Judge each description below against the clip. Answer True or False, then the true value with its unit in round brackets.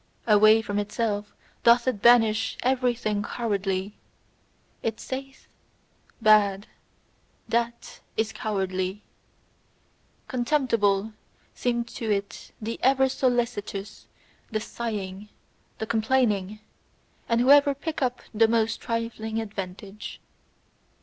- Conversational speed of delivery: False (95 wpm)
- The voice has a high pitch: True (220 Hz)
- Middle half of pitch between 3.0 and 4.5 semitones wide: False (2.6 semitones)